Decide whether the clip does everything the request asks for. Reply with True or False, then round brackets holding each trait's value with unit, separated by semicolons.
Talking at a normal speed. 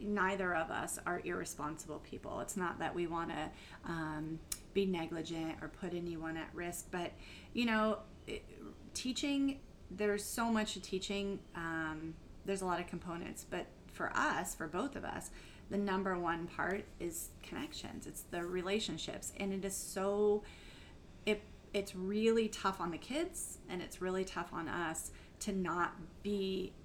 True (160 wpm)